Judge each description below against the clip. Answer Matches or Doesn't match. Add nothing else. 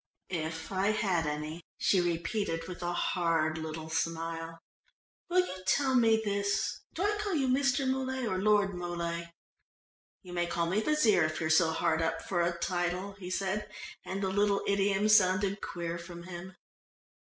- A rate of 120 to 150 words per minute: Doesn't match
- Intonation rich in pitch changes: Doesn't match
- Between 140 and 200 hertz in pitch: Matches